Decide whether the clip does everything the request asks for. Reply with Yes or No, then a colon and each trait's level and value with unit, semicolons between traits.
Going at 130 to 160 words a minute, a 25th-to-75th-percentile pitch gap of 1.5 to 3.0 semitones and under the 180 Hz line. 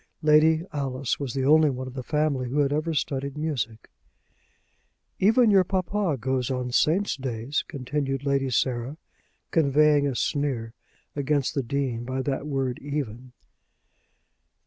Yes: average, 140 wpm; average, 2.7 semitones; medium, 140 Hz